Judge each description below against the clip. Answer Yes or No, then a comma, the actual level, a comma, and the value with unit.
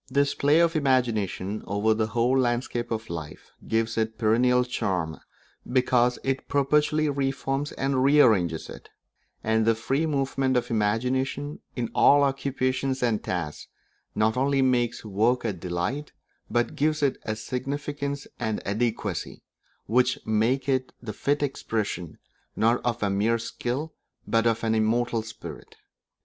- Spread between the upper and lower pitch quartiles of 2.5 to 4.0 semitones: Yes, average, 3.7 semitones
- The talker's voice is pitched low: Yes, low, 120 Hz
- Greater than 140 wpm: Yes, average, 150 wpm